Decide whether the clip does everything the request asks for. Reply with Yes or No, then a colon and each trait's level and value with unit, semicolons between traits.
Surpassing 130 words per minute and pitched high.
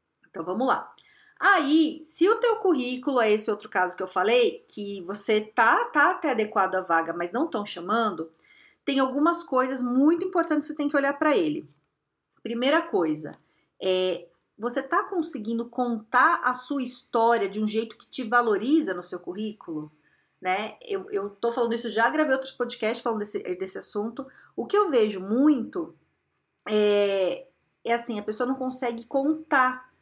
Yes: average, 170 wpm; very high, 250 Hz